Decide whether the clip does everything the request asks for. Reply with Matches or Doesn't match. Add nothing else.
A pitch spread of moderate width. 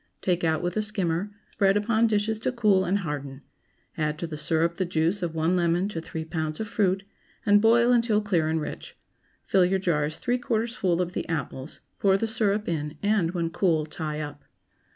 Matches